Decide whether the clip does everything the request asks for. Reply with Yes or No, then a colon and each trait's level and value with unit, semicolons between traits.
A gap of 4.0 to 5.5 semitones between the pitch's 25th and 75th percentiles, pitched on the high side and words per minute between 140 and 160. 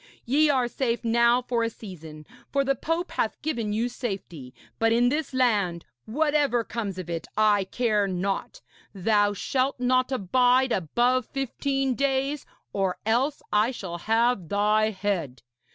Yes: average, 4.4 semitones; high, 230 Hz; average, 150 wpm